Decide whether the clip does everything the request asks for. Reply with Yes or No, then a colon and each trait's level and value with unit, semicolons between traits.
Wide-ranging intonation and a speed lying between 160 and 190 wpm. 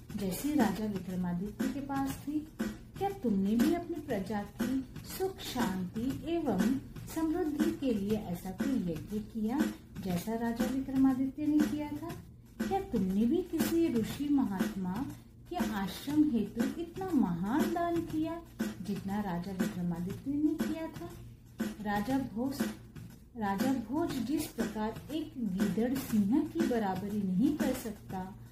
No: wide, 6.2 semitones; average, 130 wpm